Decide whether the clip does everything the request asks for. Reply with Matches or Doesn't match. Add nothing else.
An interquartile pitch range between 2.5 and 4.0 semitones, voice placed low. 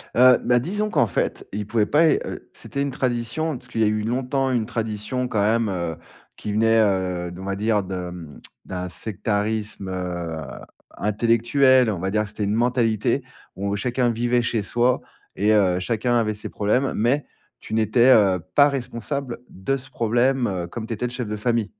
Matches